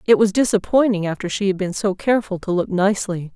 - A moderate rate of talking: No, fast, 215 wpm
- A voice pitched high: Yes, high, 200 Hz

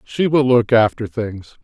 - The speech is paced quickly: No, average, 185 wpm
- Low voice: Yes, low, 115 Hz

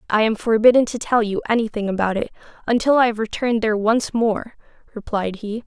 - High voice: Yes, high, 225 Hz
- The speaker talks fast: No, average, 190 wpm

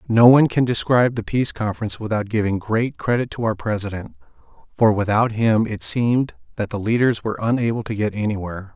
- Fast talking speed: No, average, 185 wpm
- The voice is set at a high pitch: No, low, 110 Hz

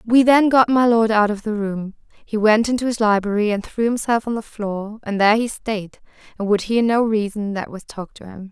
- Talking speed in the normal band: No, fast, 240 wpm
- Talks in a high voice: Yes, high, 215 Hz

